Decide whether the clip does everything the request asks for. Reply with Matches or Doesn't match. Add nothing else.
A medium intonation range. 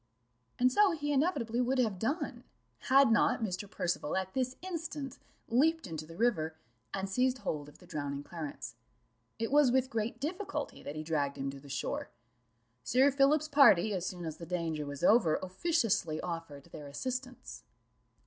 Doesn't match